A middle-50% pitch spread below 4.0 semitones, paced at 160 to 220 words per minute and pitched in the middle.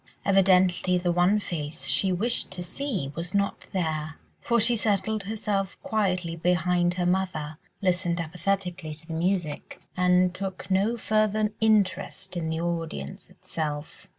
No: average, 2.8 semitones; average, 145 wpm; medium, 180 Hz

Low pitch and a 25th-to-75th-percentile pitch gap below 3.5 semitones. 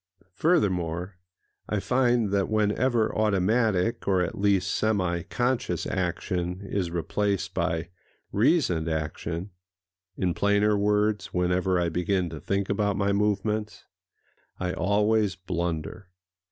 Yes: low, 100 Hz; average, 2.9 semitones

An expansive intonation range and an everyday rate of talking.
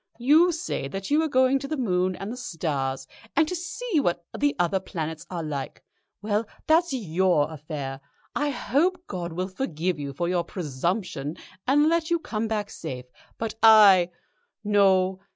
Yes: wide, 8.5 semitones; average, 170 wpm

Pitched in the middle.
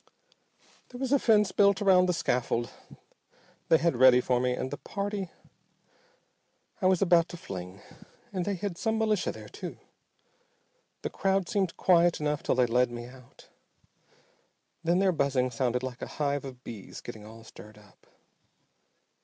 Yes: medium, 150 Hz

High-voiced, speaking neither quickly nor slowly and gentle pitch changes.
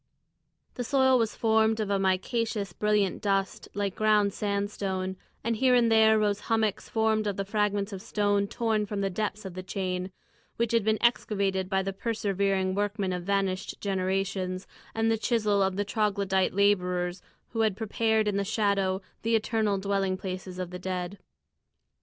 Yes: high, 200 Hz; average, 170 wpm; narrow, 2.3 semitones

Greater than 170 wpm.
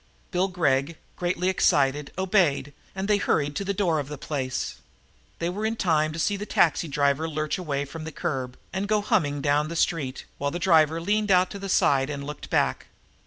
Yes: average, 200 wpm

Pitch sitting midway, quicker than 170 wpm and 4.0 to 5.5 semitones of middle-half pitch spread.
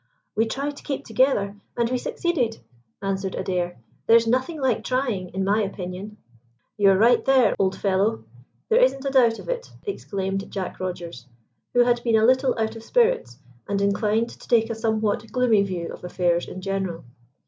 No: high, 220 Hz; average, 180 wpm; average, 4.6 semitones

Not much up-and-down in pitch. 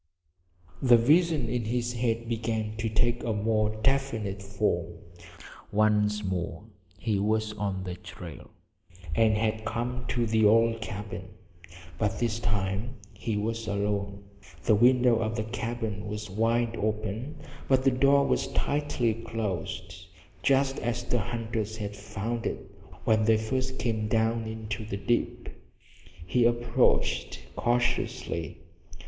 Yes: narrow, 2.3 semitones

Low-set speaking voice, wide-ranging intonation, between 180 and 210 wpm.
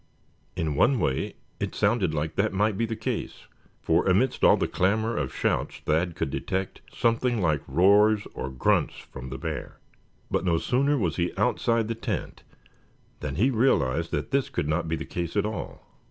Yes: very low, 95 Hz; wide, 6.3 semitones; average, 185 wpm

